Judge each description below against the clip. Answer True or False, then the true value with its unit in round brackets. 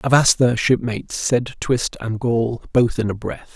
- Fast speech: False (185 wpm)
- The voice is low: True (120 Hz)